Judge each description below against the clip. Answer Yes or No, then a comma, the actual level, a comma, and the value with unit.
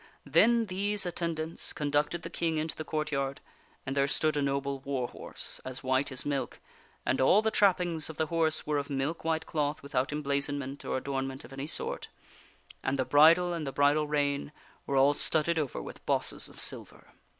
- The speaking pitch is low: No, medium, 145 Hz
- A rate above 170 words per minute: Yes, average, 190 wpm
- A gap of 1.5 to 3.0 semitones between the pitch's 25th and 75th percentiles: Yes, average, 2.7 semitones